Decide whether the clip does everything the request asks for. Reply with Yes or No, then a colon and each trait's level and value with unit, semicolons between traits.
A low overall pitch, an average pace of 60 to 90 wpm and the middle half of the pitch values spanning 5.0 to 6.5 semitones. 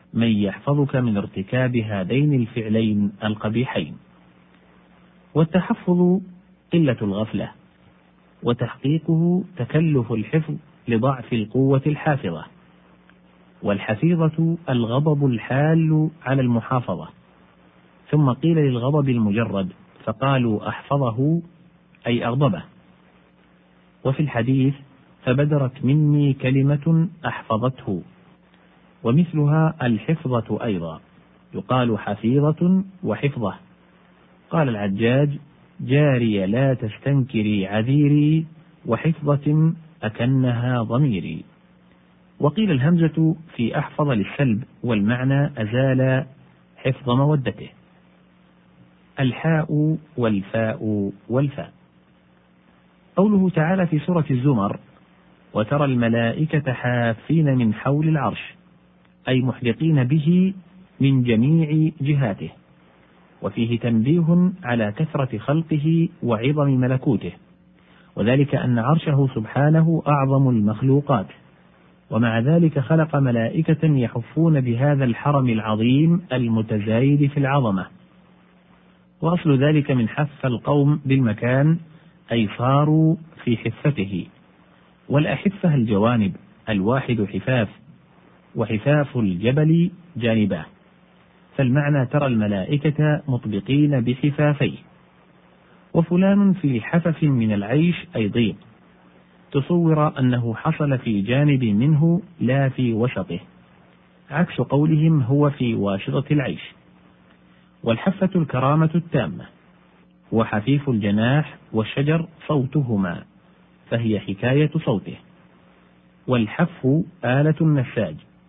Yes: low, 130 Hz; average, 80 wpm; wide, 5.6 semitones